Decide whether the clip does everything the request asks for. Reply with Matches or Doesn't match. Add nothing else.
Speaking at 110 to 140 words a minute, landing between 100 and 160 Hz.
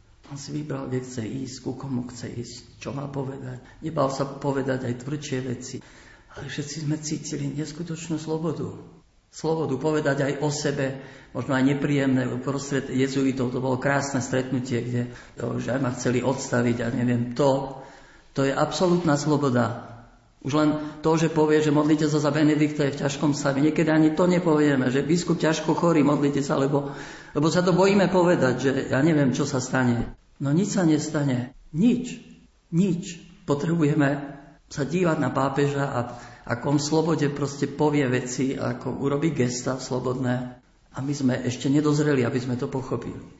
Doesn't match